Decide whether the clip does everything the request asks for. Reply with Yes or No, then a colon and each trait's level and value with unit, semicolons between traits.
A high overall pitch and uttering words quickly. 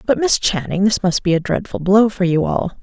Yes: high, 195 Hz; fast, 255 wpm